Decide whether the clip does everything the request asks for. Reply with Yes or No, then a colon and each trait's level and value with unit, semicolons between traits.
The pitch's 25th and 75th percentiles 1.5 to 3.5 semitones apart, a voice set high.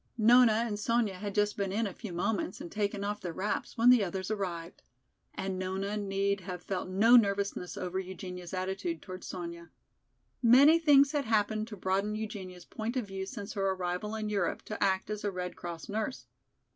Yes: average, 2.7 semitones; high, 200 Hz